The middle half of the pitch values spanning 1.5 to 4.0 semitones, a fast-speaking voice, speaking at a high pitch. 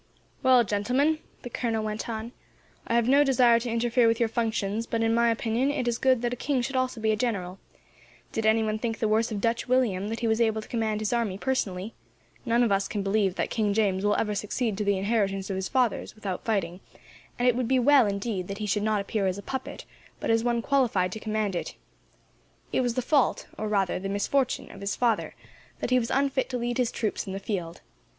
Yes: average, 3.0 semitones; fast, 230 wpm; high, 225 Hz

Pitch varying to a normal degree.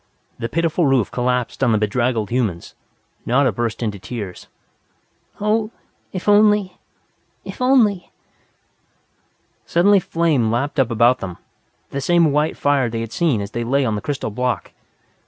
No: wide, 6.6 semitones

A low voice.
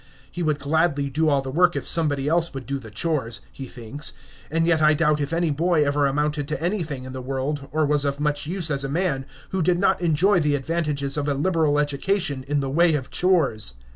No: medium, 150 Hz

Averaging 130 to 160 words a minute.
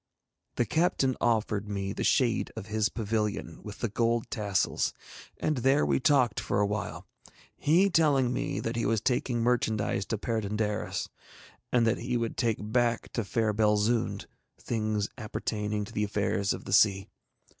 Yes: average, 155 wpm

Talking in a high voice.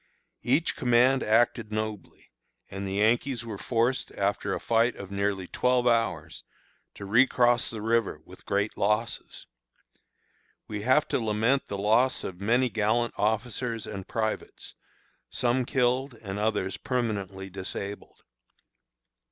No: low, 110 Hz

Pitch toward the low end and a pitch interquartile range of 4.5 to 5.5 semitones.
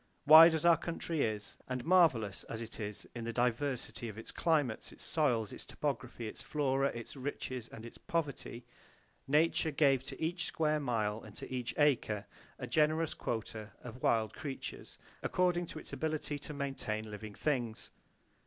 Yes: low, 130 Hz; average, 5.2 semitones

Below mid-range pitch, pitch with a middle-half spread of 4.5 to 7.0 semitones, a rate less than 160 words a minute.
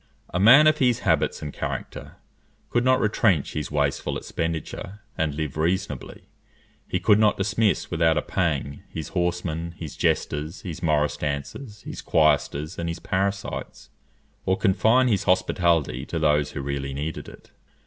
Yes: very low, 85 Hz; average, 5.0 semitones; average, 150 wpm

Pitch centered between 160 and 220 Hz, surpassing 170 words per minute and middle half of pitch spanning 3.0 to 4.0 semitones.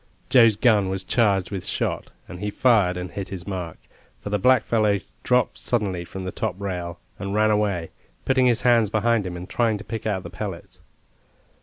No: low, 100 Hz; average, 190 wpm; average, 3.3 semitones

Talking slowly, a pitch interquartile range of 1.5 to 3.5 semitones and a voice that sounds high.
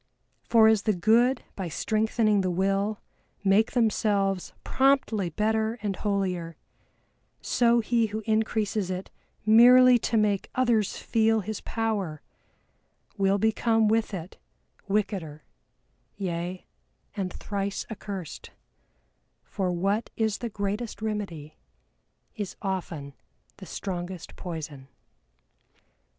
Yes: slow, 105 wpm; average, 3.0 semitones; high, 205 Hz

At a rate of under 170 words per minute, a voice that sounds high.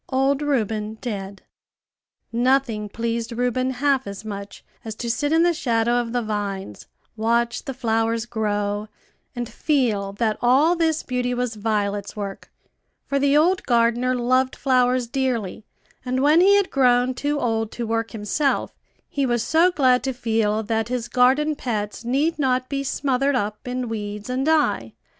Yes: average, 160 wpm; high, 245 Hz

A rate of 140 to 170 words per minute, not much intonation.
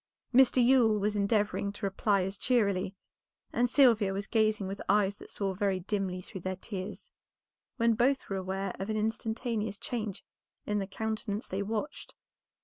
Yes: average, 160 wpm; narrow, 2.3 semitones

